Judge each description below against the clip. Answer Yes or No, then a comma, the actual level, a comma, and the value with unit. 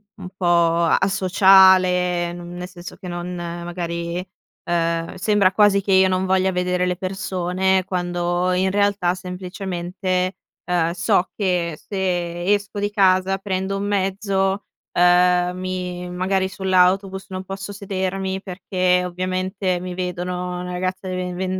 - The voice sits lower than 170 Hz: No, medium, 185 Hz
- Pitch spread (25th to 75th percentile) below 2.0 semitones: Yes, narrow, 1.2 semitones